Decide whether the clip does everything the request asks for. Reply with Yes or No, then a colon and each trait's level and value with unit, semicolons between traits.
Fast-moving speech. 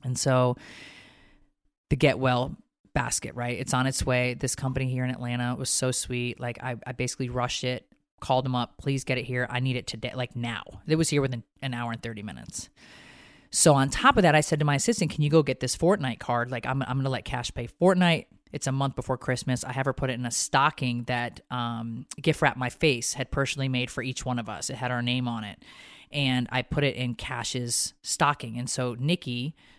Yes: fast, 235 wpm